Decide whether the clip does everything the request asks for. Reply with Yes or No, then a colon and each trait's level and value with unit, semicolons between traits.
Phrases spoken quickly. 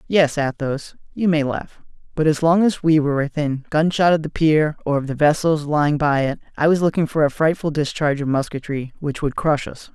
Yes: fast, 215 wpm